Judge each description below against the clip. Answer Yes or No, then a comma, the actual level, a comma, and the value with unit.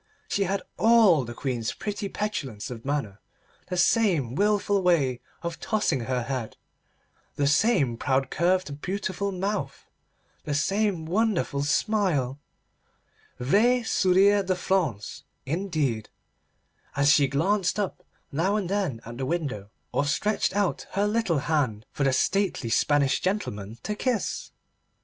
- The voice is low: No, medium, 170 Hz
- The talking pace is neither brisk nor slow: No, slow, 125 wpm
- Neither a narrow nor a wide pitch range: No, wide, 6.9 semitones